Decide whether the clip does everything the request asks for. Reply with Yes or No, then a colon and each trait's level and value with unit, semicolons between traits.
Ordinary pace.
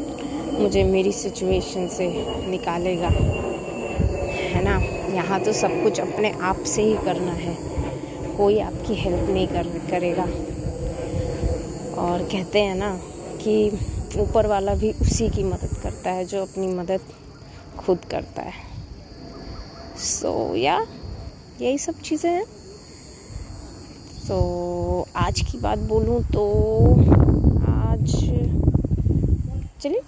Yes: average, 120 wpm